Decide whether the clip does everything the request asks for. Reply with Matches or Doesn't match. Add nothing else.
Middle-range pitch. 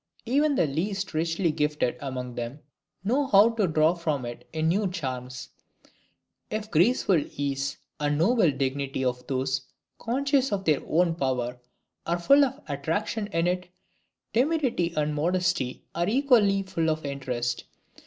Matches